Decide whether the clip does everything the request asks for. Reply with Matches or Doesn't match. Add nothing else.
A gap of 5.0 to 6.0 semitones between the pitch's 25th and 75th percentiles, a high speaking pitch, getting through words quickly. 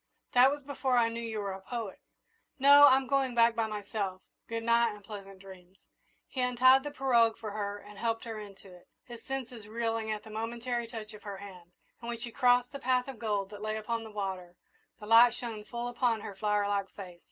Doesn't match